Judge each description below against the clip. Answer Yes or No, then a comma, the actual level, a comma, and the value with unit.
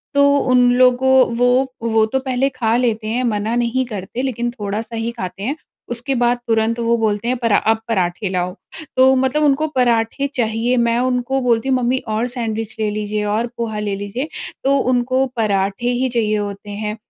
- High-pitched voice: Yes, high, 235 Hz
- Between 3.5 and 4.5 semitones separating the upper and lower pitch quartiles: No, average, 2.8 semitones